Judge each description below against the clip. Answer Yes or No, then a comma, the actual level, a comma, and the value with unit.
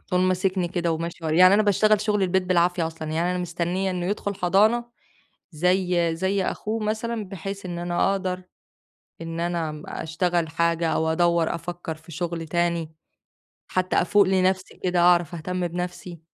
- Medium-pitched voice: Yes, medium, 175 Hz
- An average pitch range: No, narrow, 2.0 semitones